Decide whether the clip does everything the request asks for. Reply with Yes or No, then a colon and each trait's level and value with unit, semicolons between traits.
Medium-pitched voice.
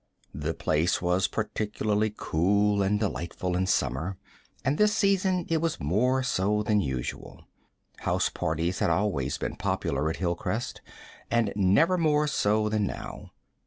No: low, 105 Hz